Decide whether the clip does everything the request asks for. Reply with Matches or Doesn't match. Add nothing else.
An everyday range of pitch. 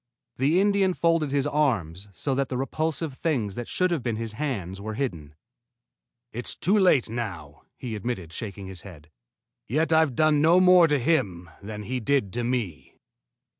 Doesn't match